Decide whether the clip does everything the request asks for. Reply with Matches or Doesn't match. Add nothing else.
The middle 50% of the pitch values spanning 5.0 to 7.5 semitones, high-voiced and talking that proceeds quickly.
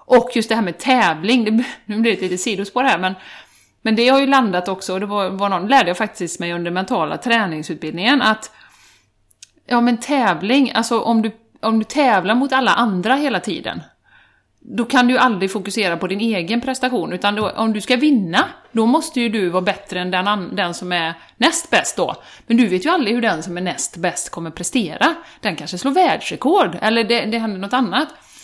Matches